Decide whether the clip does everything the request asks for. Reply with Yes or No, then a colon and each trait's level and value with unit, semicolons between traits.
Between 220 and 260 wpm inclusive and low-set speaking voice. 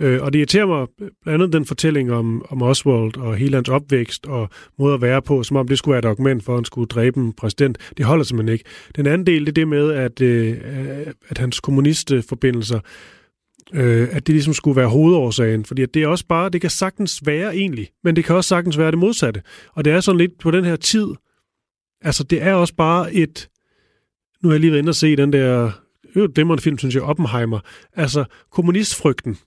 No: fast, 225 wpm; medium, 145 Hz